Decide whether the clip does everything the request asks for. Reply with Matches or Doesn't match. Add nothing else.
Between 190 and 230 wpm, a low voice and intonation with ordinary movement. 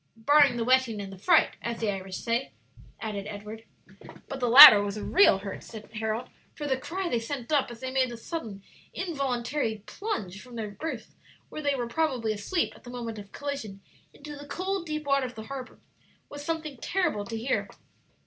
Doesn't match